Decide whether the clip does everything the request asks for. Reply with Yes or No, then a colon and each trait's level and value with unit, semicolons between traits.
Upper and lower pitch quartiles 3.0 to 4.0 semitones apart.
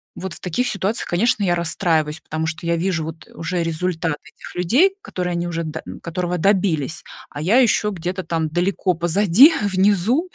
Yes: average, 3.3 semitones